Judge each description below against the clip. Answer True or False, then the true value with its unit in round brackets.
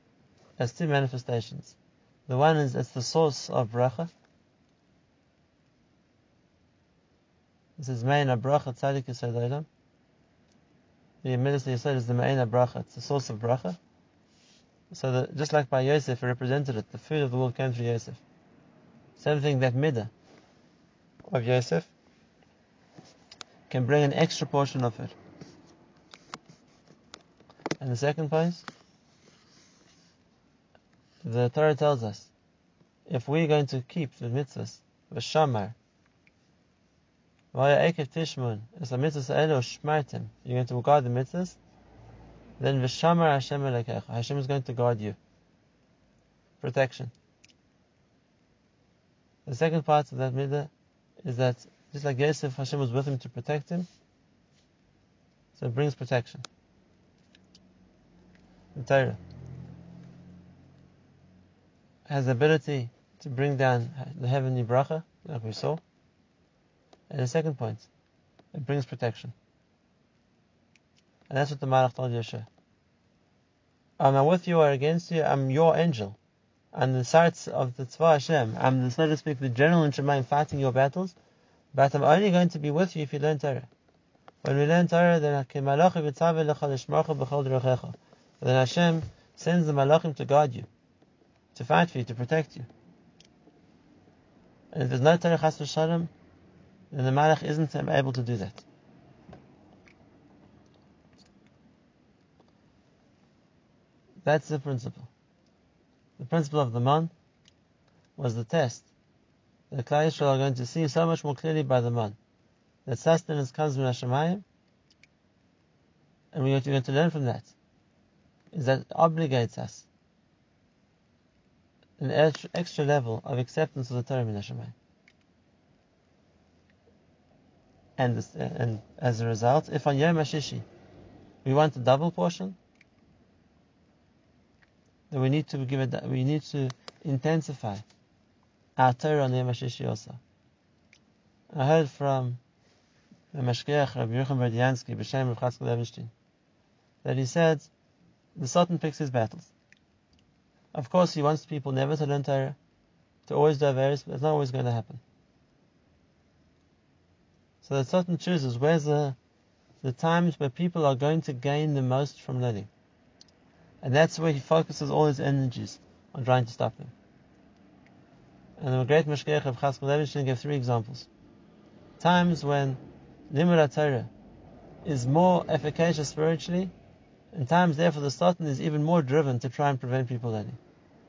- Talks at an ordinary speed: False (130 wpm)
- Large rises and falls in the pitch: False (3.6 semitones)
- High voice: False (140 Hz)